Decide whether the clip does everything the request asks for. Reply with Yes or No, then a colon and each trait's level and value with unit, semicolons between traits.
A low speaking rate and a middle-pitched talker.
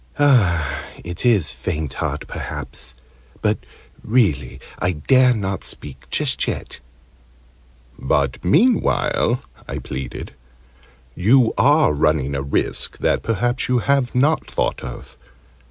No: slow, 110 wpm; very low, 95 Hz